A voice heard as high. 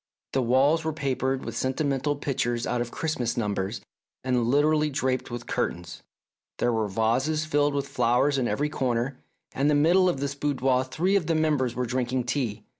No: low, 130 Hz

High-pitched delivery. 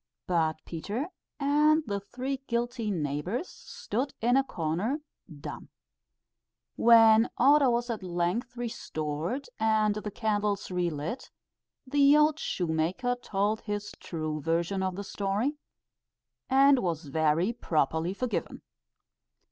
Yes: high, 210 Hz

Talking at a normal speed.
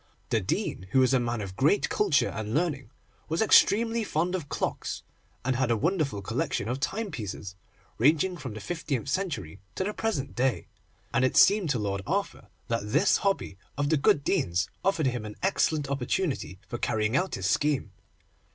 Yes: average, 180 wpm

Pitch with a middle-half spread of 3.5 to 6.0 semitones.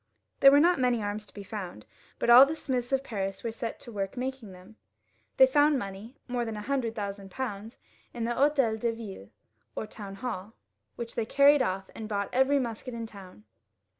Yes: average, 4.4 semitones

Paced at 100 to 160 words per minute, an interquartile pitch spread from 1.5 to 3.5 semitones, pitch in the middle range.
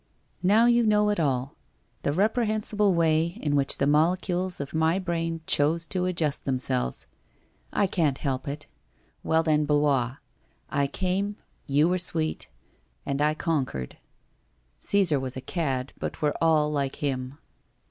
No: average, 155 wpm; average, 4.5 semitones; medium, 155 Hz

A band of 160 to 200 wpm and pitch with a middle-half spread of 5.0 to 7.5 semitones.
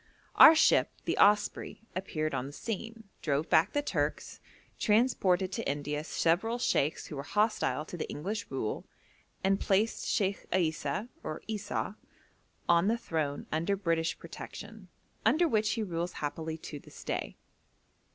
No: average, 145 wpm; wide, 5.6 semitones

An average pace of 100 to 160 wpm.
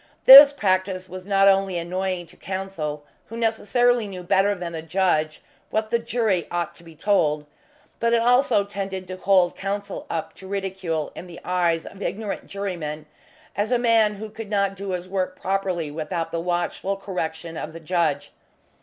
No: average, 175 wpm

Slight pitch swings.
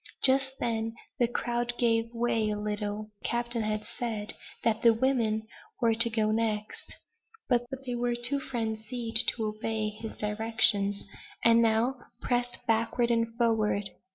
Yes: narrow, 1.8 semitones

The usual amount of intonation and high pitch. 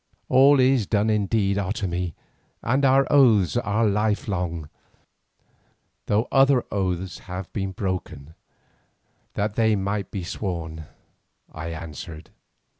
No: average, 3.8 semitones; low, 100 Hz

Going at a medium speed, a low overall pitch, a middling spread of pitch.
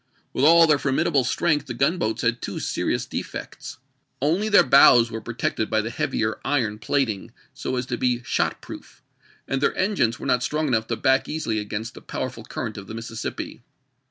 Yes: average, 185 wpm; low, 125 Hz; average, 4.4 semitones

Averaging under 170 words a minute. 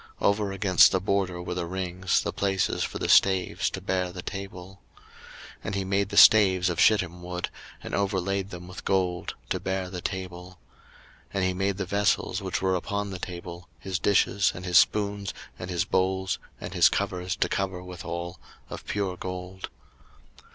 No: average, 185 wpm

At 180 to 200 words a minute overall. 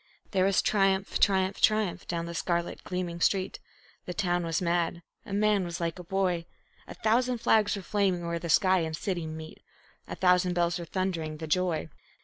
Yes: average, 185 wpm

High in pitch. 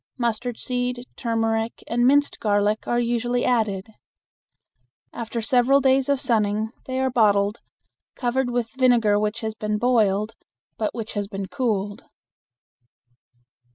Yes: high, 230 Hz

